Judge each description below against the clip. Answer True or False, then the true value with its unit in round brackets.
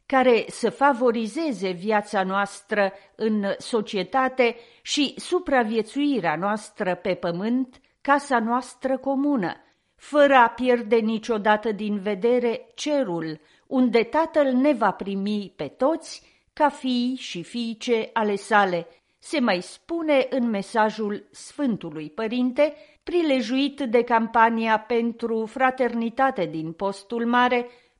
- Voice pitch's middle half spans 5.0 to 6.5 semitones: False (4.0 semitones)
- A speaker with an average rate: False (105 wpm)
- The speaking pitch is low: False (235 Hz)